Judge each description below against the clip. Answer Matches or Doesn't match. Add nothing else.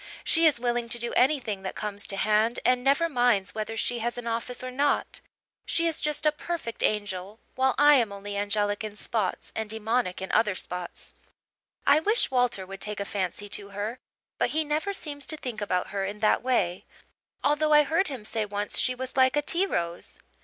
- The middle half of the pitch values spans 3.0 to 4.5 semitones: Doesn't match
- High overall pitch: Matches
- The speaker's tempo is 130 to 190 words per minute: Doesn't match